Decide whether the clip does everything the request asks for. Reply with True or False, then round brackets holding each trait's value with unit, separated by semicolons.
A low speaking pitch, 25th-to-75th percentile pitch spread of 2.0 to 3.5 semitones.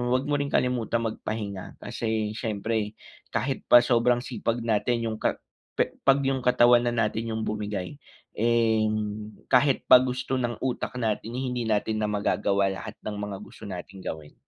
True (115 Hz; 2.7 semitones)